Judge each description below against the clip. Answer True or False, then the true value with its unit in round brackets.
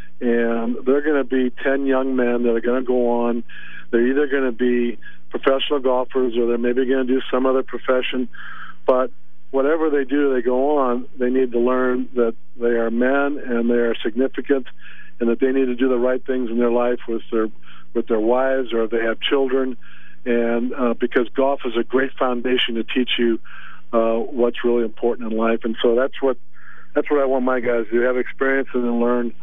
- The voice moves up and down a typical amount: False (1.8 semitones)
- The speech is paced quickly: True (210 wpm)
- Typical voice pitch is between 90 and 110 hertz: False (125 Hz)